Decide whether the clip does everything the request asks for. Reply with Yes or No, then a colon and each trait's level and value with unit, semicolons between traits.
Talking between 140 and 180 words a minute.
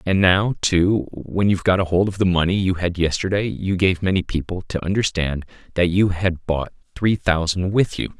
No: average, 200 wpm